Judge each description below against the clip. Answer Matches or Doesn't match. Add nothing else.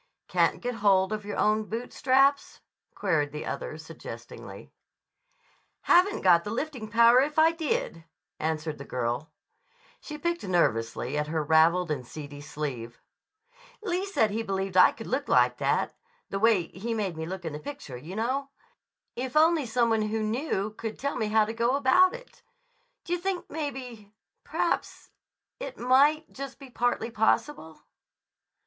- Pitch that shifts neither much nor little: Doesn't match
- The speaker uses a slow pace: Doesn't match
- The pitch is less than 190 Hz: Doesn't match